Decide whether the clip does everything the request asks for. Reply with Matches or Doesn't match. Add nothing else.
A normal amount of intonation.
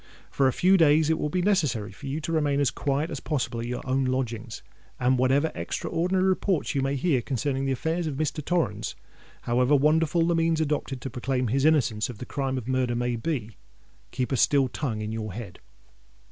Matches